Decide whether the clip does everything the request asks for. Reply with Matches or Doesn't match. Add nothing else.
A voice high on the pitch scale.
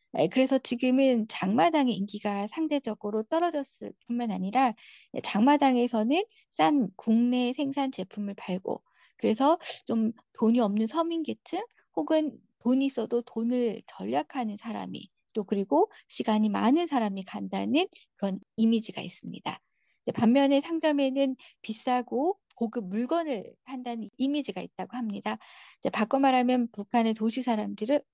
Matches